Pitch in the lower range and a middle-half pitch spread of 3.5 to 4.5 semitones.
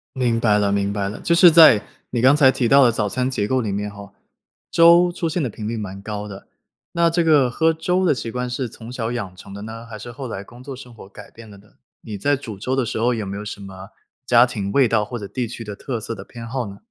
Yes: low, 115 Hz; average, 4.2 semitones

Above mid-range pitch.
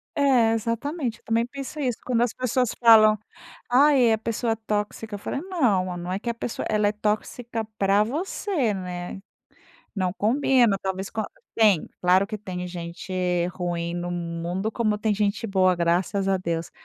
Yes: high, 215 Hz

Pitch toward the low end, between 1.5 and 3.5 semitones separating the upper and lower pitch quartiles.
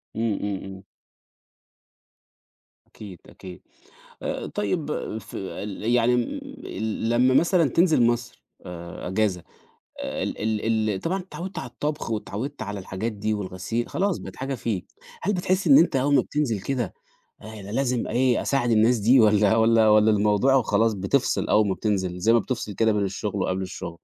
No: low, 110 Hz; average, 4.1 semitones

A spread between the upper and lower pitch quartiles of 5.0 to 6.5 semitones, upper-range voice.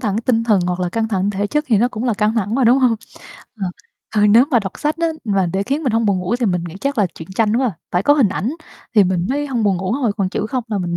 No: average, 4.2 semitones; high, 215 Hz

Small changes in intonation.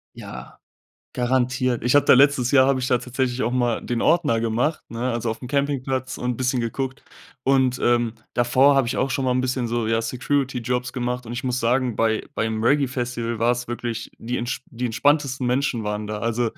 Yes: narrow, 1.8 semitones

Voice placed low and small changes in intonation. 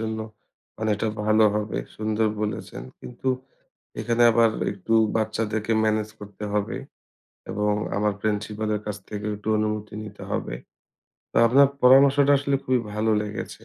Yes: low, 110 Hz; narrow, 1.4 semitones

